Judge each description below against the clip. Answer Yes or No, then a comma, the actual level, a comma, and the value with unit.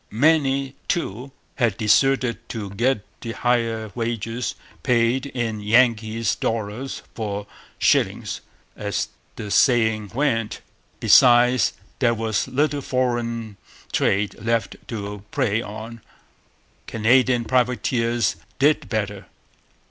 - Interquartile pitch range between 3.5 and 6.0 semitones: No, average, 2.7 semitones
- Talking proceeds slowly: Yes, slow, 100 wpm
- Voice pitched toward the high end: No, low, 115 Hz